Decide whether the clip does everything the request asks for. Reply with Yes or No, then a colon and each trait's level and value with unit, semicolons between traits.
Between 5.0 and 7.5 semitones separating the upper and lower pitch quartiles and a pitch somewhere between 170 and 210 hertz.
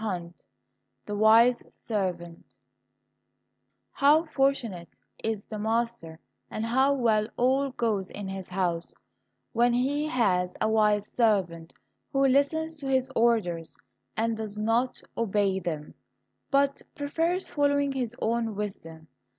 No: wide, 5.5 semitones; high, 225 Hz